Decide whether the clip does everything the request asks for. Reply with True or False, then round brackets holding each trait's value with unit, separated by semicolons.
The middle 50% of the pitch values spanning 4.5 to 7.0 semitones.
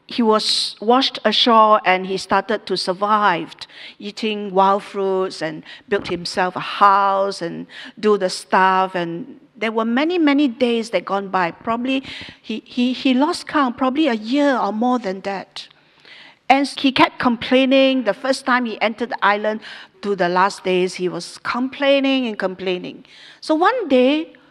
True (5.3 semitones)